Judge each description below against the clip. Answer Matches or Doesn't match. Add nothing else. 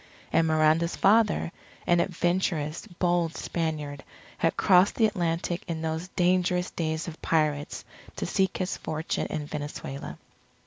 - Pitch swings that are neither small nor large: Doesn't match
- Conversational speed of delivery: Doesn't match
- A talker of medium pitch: Matches